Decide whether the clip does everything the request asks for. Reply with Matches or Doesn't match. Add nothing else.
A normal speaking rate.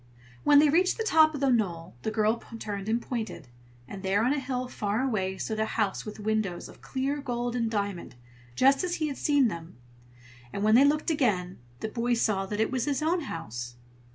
Doesn't match